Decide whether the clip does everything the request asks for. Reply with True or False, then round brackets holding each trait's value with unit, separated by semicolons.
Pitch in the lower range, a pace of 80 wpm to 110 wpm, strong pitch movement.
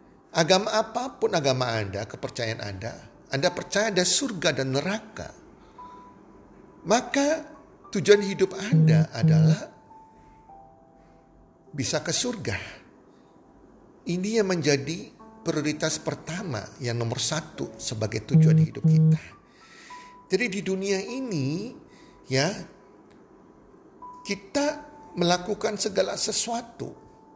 False (180 Hz; 90 wpm; 6.4 semitones)